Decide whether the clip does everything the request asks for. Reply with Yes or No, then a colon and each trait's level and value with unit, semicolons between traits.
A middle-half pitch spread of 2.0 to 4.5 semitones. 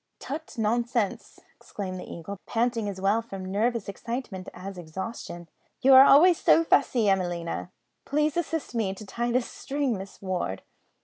No: average, 5.0 semitones